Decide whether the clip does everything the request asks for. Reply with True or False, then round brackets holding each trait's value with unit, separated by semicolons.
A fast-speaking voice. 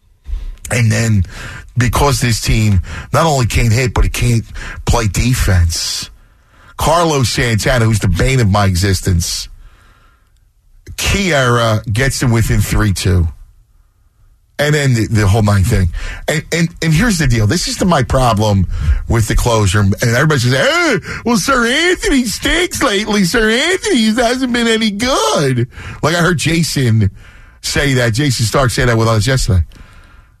False (150 wpm)